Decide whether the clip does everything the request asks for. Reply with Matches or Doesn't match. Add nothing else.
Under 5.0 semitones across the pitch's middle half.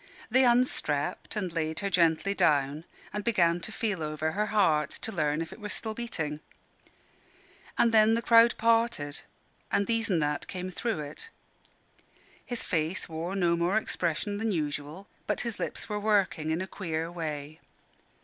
Doesn't match